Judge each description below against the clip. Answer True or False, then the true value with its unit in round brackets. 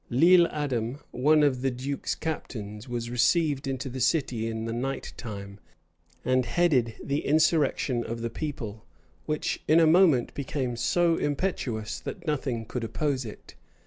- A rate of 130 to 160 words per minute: True (150 wpm)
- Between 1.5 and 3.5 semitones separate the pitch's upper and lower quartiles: False (4.5 semitones)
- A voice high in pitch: False (130 Hz)